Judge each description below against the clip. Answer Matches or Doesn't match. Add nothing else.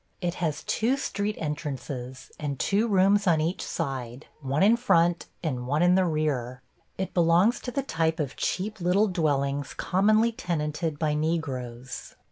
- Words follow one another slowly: Doesn't match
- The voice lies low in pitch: Doesn't match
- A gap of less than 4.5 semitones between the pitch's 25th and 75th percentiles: Doesn't match